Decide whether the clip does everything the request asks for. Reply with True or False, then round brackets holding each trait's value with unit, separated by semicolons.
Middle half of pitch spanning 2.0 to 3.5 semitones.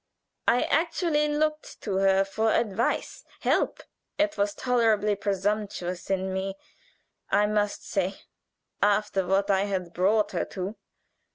True (2.5 semitones)